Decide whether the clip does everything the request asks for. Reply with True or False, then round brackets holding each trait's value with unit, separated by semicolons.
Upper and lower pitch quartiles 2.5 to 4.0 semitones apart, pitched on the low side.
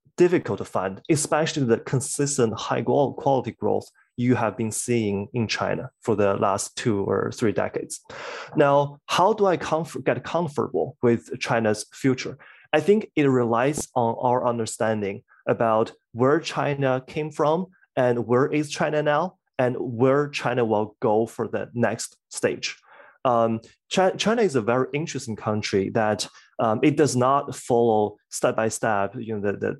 False (4.7 semitones; 125 Hz)